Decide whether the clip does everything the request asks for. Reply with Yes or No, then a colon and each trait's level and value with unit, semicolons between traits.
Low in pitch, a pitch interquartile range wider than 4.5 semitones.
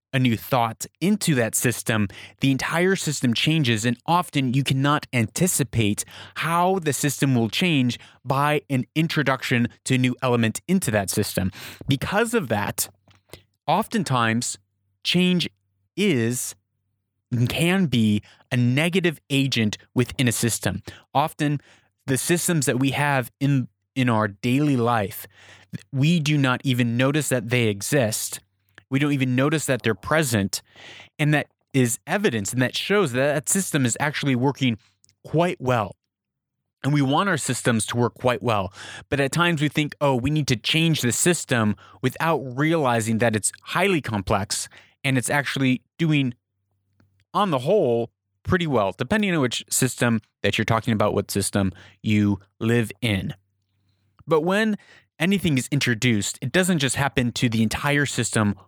Yes: low, 125 Hz; average, 5.2 semitones